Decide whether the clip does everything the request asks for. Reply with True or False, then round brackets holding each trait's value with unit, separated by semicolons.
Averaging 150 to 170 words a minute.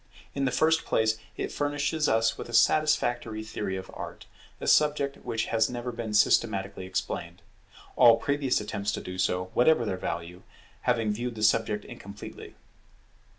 True (155 wpm)